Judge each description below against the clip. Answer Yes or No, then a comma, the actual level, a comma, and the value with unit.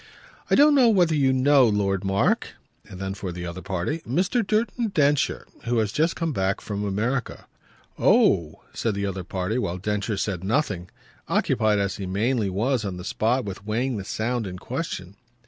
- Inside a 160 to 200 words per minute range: Yes, average, 180 wpm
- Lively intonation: Yes, wide, 5.7 semitones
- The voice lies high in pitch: No, low, 105 Hz